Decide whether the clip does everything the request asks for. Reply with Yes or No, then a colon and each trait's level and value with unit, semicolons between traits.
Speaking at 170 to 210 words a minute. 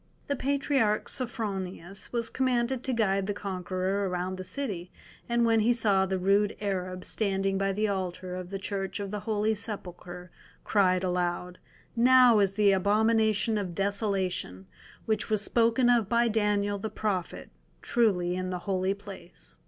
No: average, 155 wpm